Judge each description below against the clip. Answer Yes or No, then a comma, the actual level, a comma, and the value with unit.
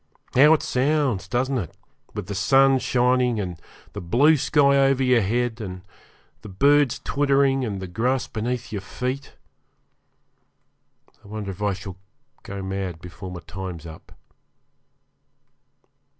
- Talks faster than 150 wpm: No, slow, 135 wpm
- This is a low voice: Yes, low, 115 Hz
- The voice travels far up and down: Yes, wide, 5.8 semitones